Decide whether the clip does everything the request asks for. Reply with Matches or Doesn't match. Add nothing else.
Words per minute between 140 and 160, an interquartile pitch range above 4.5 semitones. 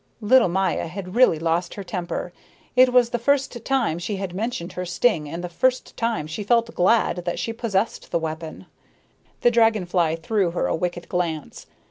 Doesn't match